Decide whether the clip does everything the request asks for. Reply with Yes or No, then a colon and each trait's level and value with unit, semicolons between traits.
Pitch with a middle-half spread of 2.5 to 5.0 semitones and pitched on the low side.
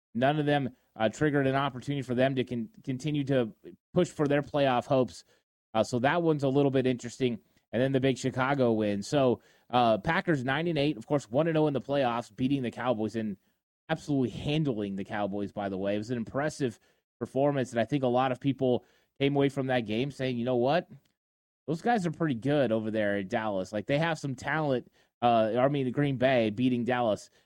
Yes: average, 3.8 semitones; low, 130 Hz